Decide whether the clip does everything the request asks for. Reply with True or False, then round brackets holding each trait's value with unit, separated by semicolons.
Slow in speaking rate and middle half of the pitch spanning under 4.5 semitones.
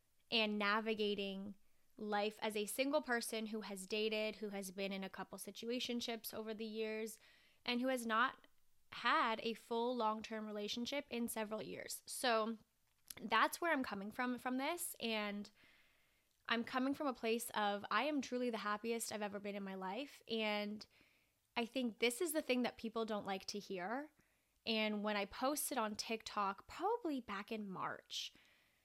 False (170 wpm; 2.7 semitones)